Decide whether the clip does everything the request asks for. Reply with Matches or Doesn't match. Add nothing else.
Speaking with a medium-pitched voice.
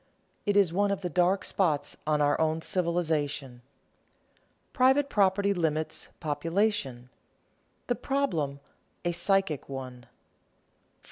Matches